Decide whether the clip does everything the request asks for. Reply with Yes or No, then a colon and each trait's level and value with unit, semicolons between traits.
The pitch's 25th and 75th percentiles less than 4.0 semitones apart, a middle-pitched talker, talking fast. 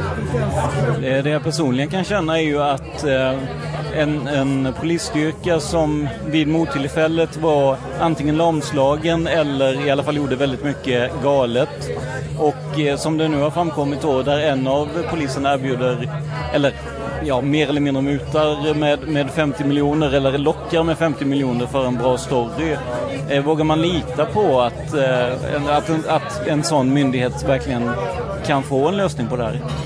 No: narrow, 2.5 semitones; medium, 145 Hz; average, 150 wpm